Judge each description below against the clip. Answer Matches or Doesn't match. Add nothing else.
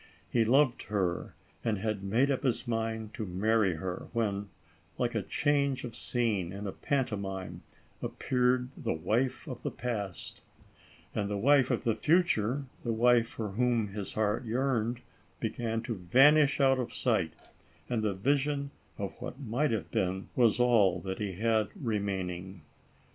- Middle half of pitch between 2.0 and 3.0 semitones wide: Doesn't match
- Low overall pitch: Matches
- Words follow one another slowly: Doesn't match